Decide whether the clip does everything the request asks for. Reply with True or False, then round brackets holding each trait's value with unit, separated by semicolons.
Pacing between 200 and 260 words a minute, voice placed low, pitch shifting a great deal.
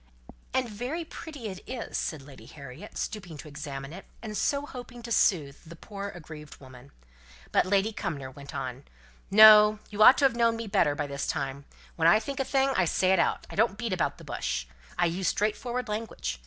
False (205 wpm; 195 Hz; 7.9 semitones)